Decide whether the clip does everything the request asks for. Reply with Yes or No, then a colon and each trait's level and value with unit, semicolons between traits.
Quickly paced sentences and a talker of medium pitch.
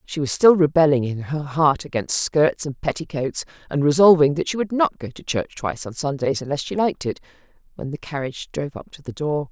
Yes: fast, 220 wpm; medium, 150 Hz